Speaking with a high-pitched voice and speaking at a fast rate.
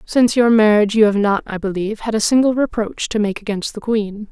Yes: high, 215 Hz; fast, 235 wpm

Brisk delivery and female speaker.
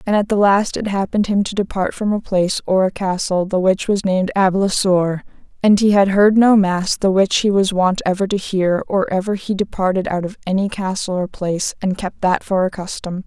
Yes: fast, 225 wpm; female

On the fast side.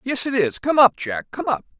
Yes: fast, 270 wpm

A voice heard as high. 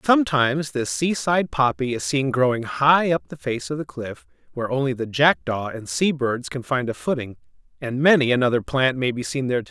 No: low, 130 Hz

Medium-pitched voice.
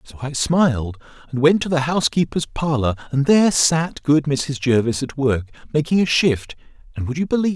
Yes: medium, 145 Hz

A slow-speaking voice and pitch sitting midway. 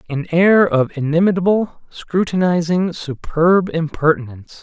Yes: slow, 90 wpm; medium, 170 Hz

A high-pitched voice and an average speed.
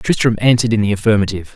No: low, 110 Hz; average, 195 wpm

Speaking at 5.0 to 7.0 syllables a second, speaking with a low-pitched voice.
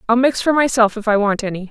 No: 6.5 syllables/s; high, 230 Hz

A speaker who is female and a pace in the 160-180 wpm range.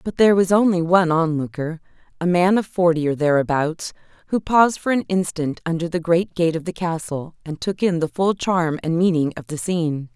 No: female; fast, 205 wpm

